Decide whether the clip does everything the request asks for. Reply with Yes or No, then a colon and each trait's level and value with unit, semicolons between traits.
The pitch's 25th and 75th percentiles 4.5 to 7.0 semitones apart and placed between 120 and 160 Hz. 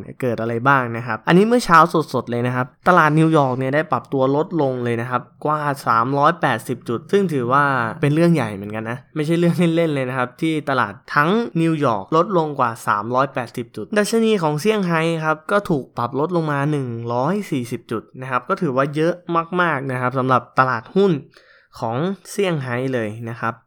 Yes: average, 5.0 semitones; medium, 140 Hz